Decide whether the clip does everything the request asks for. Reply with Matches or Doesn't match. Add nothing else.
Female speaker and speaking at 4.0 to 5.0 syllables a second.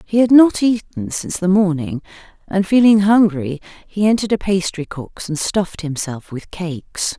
Matches